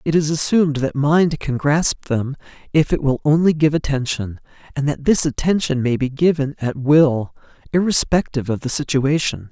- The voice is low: No, medium, 145 Hz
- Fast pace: No, average, 170 wpm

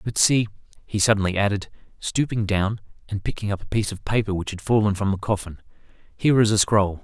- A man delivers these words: Yes, male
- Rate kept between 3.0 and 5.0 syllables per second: No, 6.2 syllables/s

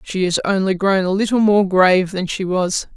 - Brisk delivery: Yes, fast, 225 wpm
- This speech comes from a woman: Yes, female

